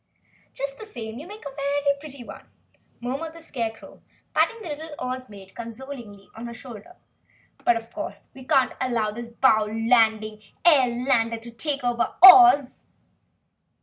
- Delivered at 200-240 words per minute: No, average, 145 wpm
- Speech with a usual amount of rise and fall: Yes, average, 3.8 semitones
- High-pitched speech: Yes, very high, 250 Hz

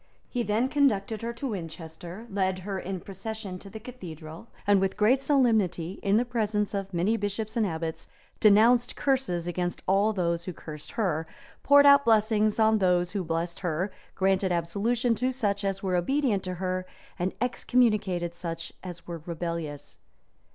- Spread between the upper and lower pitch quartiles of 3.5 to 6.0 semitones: Yes, average, 4.2 semitones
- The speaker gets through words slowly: No, average, 165 wpm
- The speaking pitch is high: Yes, high, 195 Hz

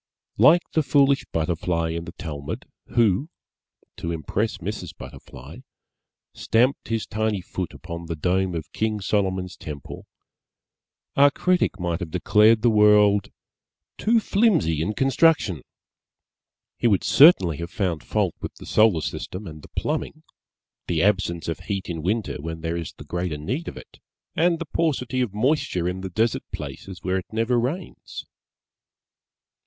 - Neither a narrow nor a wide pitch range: No, wide, 5.7 semitones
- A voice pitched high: No, very low, 95 Hz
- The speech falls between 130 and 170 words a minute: Yes, average, 150 wpm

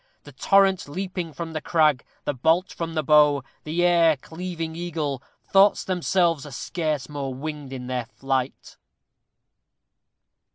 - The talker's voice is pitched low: No, medium, 160 Hz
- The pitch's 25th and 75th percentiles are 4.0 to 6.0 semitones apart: No, average, 3.5 semitones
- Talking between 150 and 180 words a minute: No, slow, 135 wpm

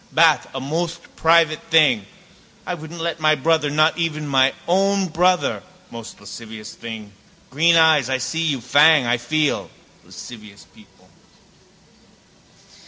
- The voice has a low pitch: No, medium, 155 Hz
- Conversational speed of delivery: No, slow, 130 wpm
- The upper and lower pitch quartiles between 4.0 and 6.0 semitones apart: Yes, average, 4.7 semitones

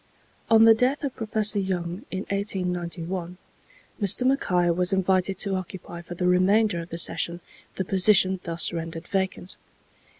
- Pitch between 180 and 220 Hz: Yes, medium, 185 Hz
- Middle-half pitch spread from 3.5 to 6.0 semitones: No, narrow, 2.6 semitones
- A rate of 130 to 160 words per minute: Yes, average, 145 wpm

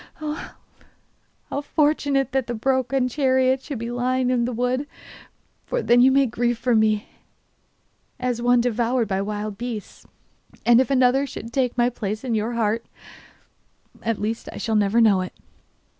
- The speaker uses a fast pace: No, average, 165 wpm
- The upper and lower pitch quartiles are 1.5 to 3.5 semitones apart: Yes, narrow, 2.6 semitones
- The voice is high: Yes, high, 245 Hz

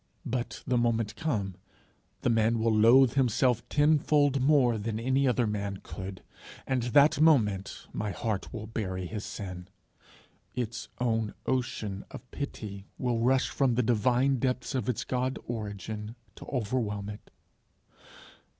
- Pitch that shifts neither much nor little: Yes, average, 3.6 semitones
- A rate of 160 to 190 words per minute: No, average, 140 wpm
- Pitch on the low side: Yes, low, 115 Hz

